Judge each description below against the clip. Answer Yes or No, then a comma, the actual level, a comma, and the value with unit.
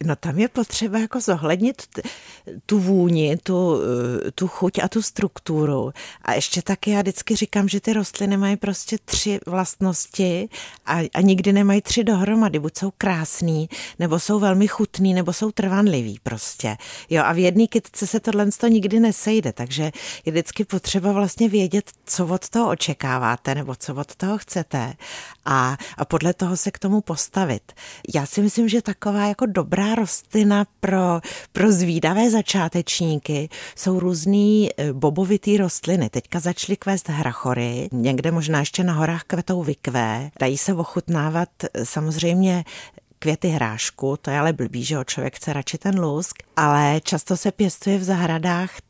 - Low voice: No, medium, 180 Hz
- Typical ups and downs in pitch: Yes, average, 4.7 semitones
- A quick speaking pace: No, average, 155 wpm